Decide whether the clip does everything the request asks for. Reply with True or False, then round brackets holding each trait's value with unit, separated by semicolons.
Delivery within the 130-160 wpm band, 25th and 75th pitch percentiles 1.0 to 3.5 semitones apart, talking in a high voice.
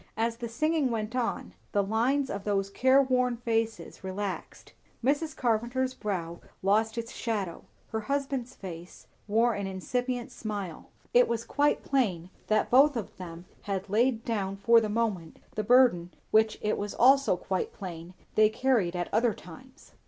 False (155 wpm; 4.2 semitones; 225 Hz)